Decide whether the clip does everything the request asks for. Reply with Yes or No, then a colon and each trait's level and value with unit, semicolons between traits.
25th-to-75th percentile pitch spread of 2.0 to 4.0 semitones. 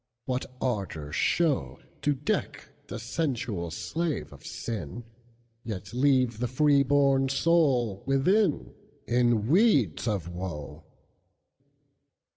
No: average, 4.8 semitones